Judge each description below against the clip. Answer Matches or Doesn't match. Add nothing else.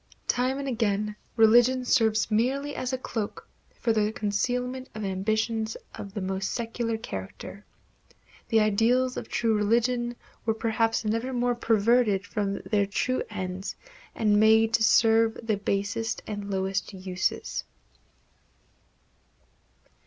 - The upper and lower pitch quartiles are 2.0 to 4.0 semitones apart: Matches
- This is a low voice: Doesn't match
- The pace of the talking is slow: Matches